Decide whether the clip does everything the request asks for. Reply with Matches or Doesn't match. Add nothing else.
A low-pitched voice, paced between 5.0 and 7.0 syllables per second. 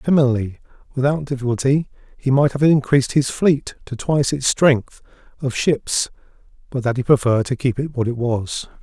Matches